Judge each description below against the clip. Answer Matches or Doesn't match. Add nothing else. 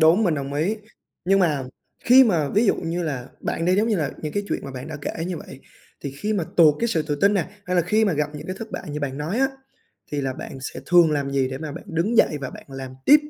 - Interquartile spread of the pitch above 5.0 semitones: Matches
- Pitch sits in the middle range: Matches